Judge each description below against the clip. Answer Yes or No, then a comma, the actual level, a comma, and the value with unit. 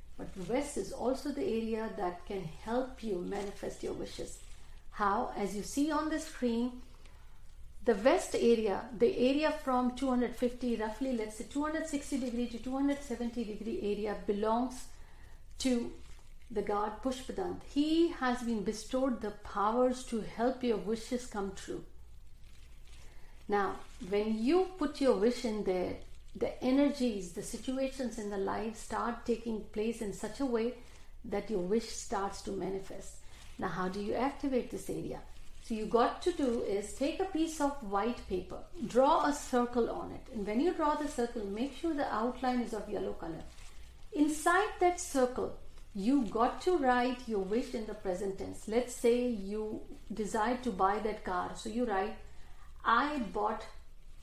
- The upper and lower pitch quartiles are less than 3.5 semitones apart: No, average, 3.8 semitones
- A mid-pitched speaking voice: No, high, 235 Hz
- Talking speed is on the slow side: No, average, 160 wpm